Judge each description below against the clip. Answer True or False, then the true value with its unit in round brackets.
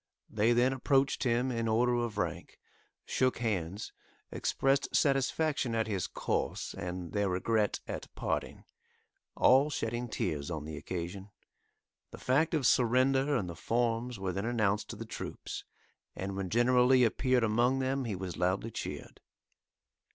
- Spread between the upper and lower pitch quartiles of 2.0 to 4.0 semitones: False (4.7 semitones)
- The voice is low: True (115 Hz)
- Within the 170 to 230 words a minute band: False (150 wpm)